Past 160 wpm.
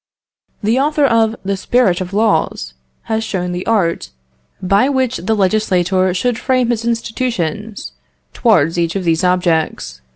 No: average, 140 wpm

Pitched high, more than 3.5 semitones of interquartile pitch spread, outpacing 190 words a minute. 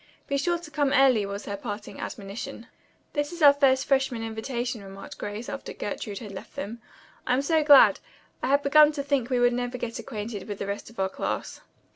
Yes: high, 245 Hz; average, 5.2 semitones; fast, 205 wpm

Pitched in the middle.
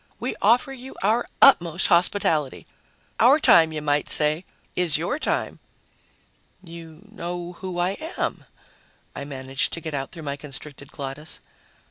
Yes: medium, 165 Hz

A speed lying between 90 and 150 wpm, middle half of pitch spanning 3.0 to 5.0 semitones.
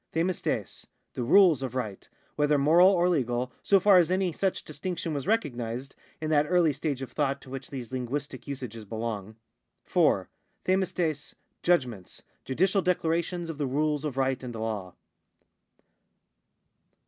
No: average, 145 wpm; wide, 5.4 semitones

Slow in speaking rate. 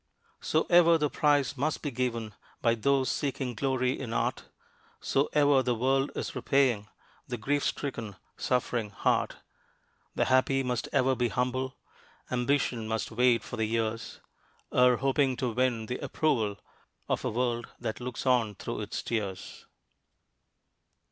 No: average, 145 wpm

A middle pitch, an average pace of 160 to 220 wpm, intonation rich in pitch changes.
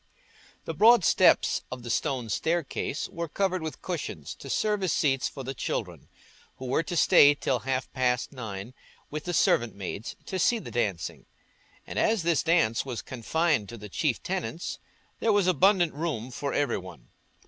Yes: medium, 145 Hz; average, 175 wpm; wide, 6.5 semitones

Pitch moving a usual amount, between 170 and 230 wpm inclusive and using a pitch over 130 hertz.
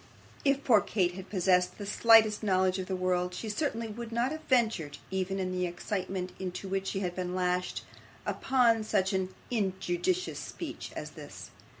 Yes: average, 3.5 semitones; average, 175 wpm; high, 190 Hz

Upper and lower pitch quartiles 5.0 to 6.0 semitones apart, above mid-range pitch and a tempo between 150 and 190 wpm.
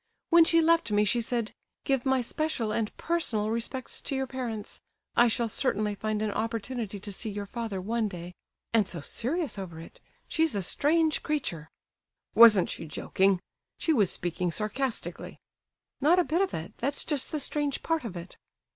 Yes: wide, 5.6 semitones; high, 230 Hz; average, 175 wpm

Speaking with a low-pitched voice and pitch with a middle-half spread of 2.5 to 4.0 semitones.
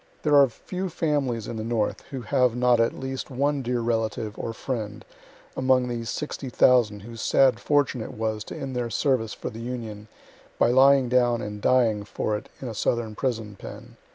Yes: low, 120 Hz; average, 2.9 semitones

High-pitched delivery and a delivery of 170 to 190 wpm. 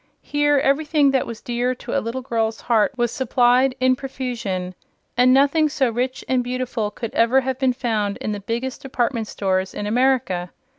Yes: very high, 250 Hz; average, 180 wpm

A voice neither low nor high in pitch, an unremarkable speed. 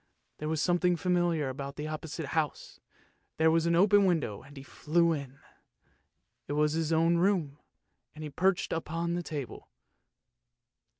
Yes: medium, 160 Hz; average, 155 wpm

